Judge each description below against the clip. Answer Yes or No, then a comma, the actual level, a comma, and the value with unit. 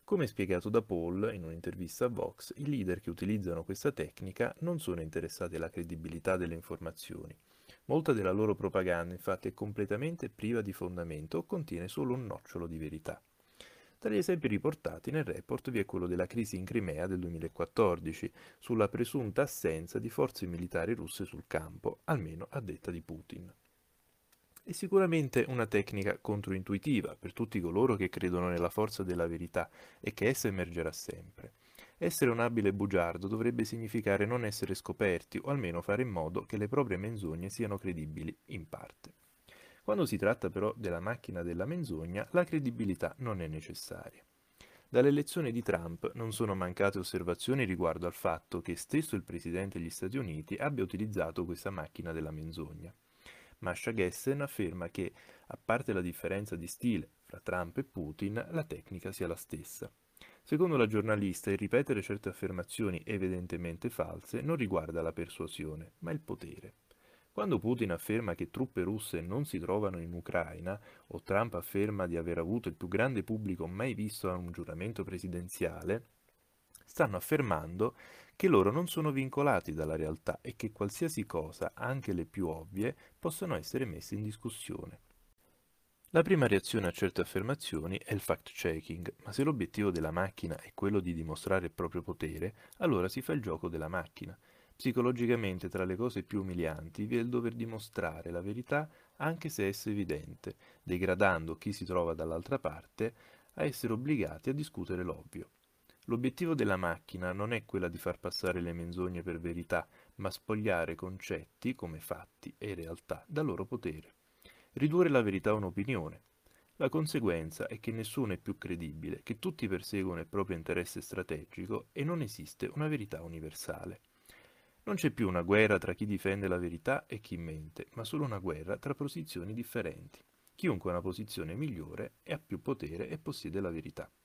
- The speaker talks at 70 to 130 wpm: No, average, 165 wpm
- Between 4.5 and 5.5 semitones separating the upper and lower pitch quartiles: Yes, average, 5.1 semitones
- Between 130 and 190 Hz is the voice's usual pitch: No, low, 100 Hz